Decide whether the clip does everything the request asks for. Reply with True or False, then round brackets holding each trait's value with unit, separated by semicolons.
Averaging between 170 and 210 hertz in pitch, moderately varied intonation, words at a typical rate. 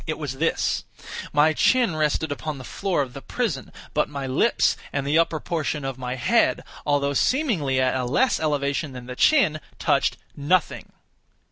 False (145 Hz; 3.1 semitones; 170 wpm)